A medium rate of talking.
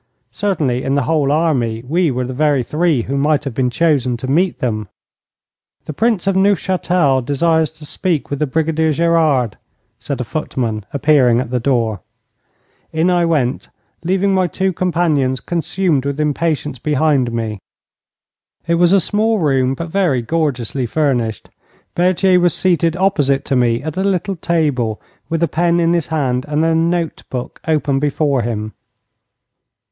Yes: average, 160 wpm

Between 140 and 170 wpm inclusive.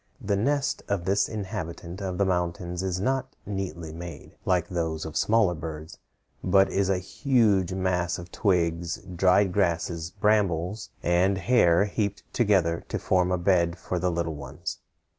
Yes: average, 155 wpm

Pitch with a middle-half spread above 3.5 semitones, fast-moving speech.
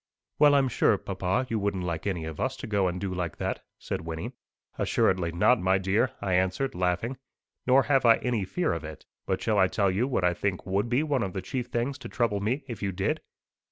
Yes: average, 5.0 semitones; fast, 230 wpm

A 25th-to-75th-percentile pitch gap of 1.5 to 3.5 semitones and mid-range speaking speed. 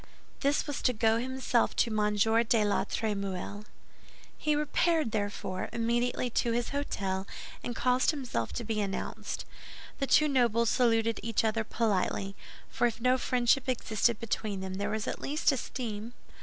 Yes: average, 3.2 semitones; average, 155 wpm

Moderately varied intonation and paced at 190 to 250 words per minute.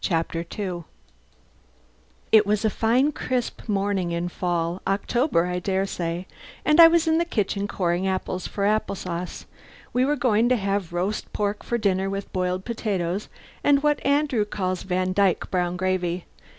No: average, 3.8 semitones; average, 160 wpm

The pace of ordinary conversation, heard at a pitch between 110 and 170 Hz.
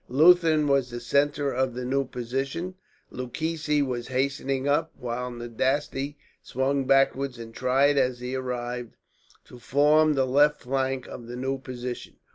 Yes: average, 145 wpm; low, 135 Hz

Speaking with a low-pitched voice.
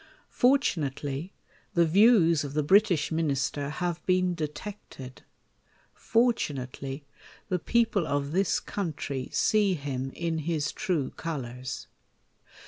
No: medium, 160 Hz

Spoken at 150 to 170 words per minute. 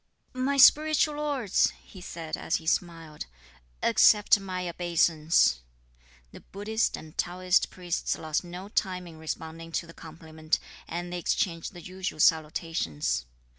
No: slow, 135 wpm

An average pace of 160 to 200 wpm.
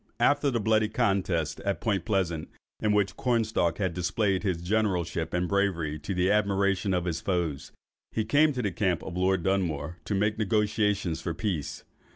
Yes: average, 180 wpm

